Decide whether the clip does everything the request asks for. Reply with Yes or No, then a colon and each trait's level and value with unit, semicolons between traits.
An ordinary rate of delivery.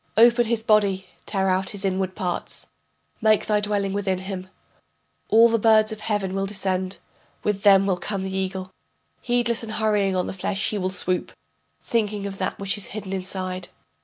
Yes: average, 180 wpm